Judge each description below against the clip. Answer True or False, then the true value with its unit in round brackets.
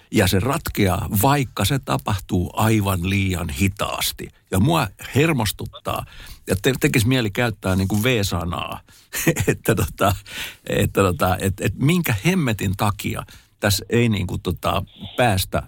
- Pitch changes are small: False (4.1 semitones)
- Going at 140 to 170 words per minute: False (130 wpm)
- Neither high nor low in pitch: False (105 Hz)